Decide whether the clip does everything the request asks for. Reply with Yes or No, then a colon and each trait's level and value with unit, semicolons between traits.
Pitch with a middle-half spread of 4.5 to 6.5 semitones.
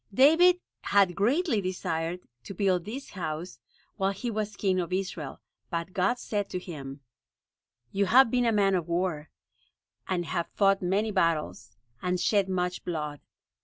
No: average, 3.3 semitones